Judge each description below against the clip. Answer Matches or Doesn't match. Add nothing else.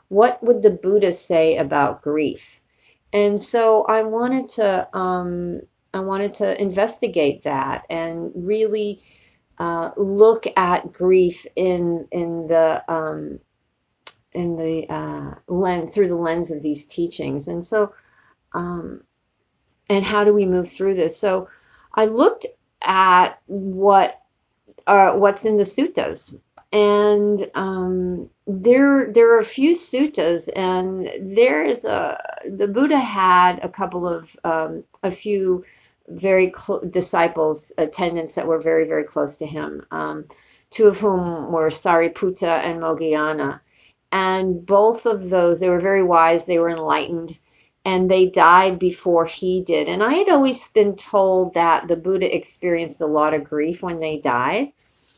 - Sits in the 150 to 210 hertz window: Matches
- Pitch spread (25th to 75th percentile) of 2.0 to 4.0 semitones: Matches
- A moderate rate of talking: Matches